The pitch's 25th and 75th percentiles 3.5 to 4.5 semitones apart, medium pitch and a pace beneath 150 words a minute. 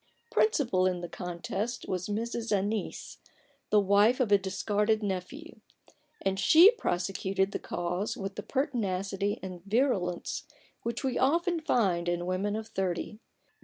No: average, 4.2 semitones; high, 200 Hz; slow, 135 wpm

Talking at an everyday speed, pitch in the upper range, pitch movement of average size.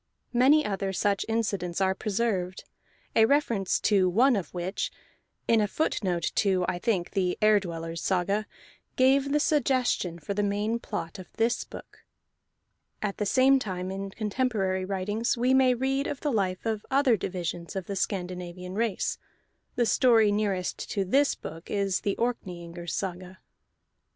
Yes: average, 155 wpm; high, 200 Hz; average, 4.1 semitones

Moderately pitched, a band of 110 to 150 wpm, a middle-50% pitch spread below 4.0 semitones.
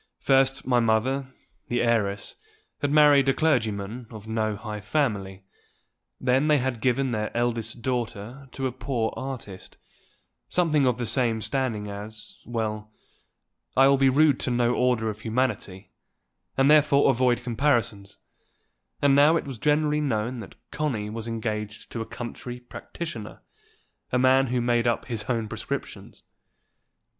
No: low, 120 Hz; average, 145 wpm; average, 3.5 semitones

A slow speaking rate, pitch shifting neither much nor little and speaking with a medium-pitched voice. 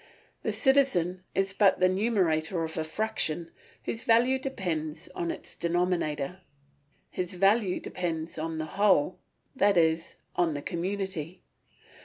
Yes: slow, 130 wpm; average, 3.6 semitones; medium, 180 Hz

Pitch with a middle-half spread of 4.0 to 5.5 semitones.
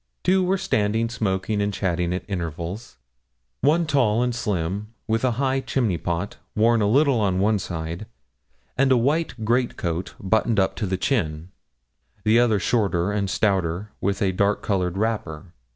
Yes: average, 4.3 semitones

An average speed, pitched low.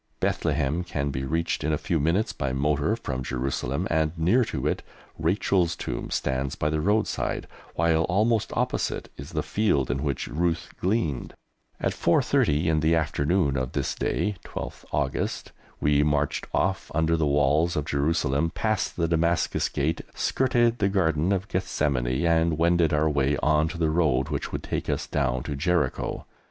Yes: average, 170 wpm; very low, 80 Hz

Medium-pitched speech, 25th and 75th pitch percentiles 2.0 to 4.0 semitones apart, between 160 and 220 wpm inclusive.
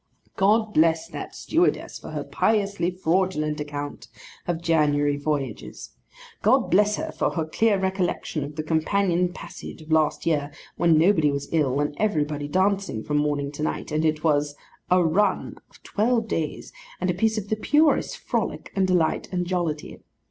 No: medium, 165 Hz; average, 4.4 semitones; average, 165 wpm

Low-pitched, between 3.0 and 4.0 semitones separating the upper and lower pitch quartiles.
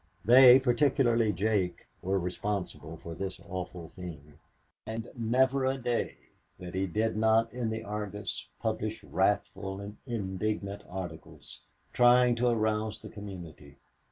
Yes: low, 105 Hz; average, 3.7 semitones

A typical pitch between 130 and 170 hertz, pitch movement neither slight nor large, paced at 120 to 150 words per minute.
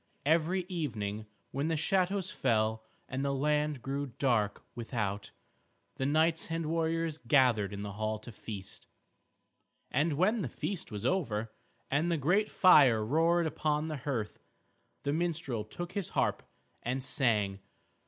No: medium, 140 Hz; wide, 6.6 semitones; average, 145 wpm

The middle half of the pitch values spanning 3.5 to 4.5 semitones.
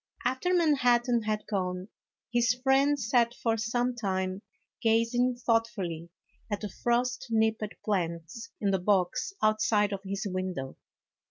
Yes: average, 3.9 semitones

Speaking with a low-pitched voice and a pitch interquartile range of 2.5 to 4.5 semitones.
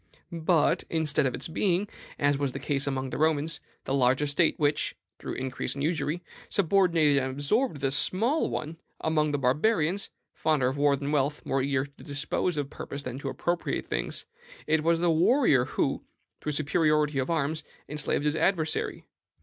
No: medium, 150 Hz; average, 2.8 semitones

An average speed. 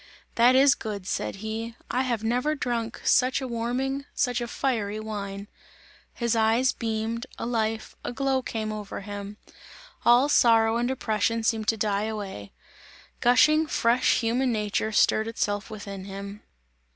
Yes: average, 150 wpm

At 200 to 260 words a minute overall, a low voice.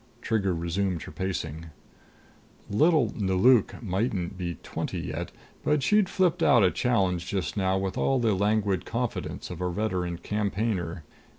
No: average, 140 wpm; very low, 95 Hz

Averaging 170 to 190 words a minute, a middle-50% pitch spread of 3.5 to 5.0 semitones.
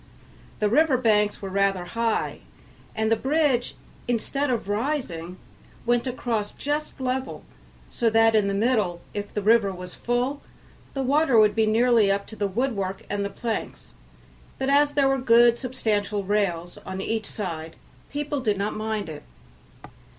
No: average, 155 wpm; average, 4.1 semitones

